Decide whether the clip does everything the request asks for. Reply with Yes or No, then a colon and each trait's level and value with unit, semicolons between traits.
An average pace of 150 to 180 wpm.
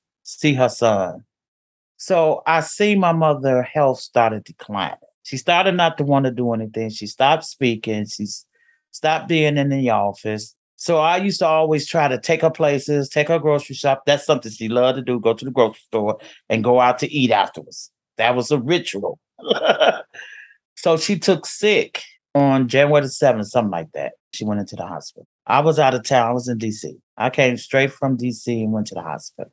No: average, 200 wpm